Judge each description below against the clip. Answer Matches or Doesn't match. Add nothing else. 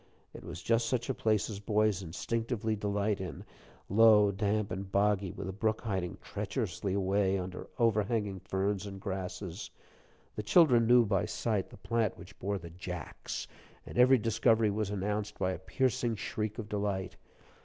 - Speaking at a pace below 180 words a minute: Matches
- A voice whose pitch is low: Matches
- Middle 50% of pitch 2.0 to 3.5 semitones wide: Matches